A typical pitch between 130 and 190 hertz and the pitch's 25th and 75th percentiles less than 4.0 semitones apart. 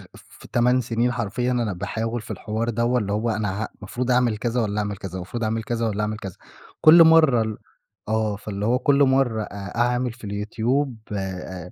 No: low, 115 Hz; average, 2.9 semitones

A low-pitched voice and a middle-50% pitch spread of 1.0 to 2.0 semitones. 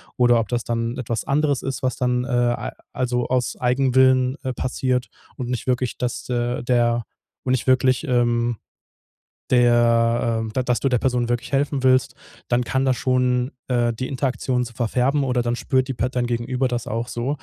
Yes: low, 125 Hz; narrow, 1.4 semitones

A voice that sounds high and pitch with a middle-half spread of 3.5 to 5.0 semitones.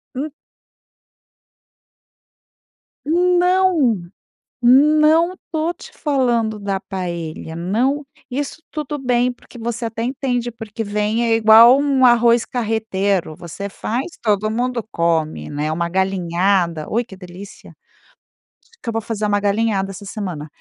Yes: high, 225 Hz; average, 4.7 semitones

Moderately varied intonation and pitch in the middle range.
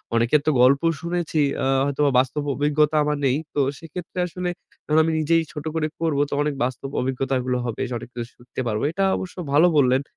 Yes: average, 3.4 semitones; medium, 145 Hz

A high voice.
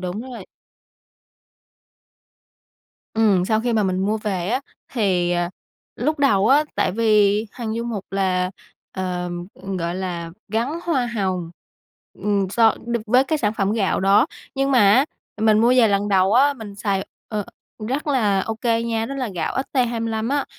Yes: high, 215 Hz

